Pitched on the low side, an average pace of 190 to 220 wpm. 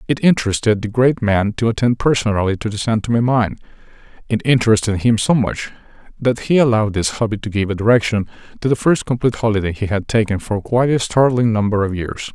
Yes: low, 110 Hz; fast, 205 wpm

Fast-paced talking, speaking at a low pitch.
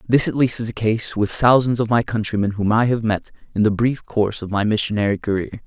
Yes: fast, 245 wpm; low, 110 Hz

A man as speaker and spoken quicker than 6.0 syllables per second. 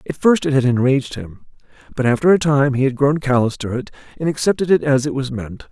Yes: male; 6.2 syllables/s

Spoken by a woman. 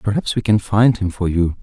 No: male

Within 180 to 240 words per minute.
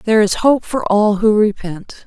Yes: fast, 205 wpm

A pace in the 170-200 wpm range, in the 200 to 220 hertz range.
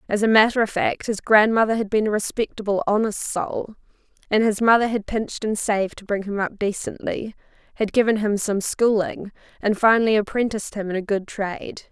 Yes: average, 190 wpm; high, 210 Hz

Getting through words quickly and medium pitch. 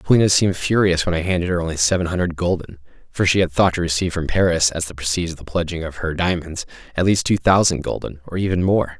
No: fast, 240 wpm; very low, 85 Hz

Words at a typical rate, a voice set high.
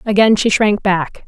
Yes: average, 190 wpm; high, 205 Hz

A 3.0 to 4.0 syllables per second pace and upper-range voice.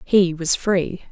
No: 3.1 syllables/s; medium, 180 Hz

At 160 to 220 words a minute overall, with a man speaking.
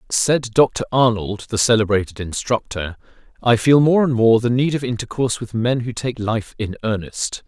Yes: average, 175 wpm; male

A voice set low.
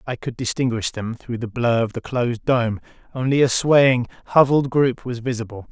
Yes: low, 120 Hz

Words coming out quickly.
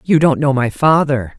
Yes: fast, 215 wpm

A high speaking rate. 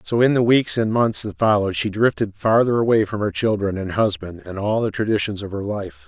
Yes: fast, 235 wpm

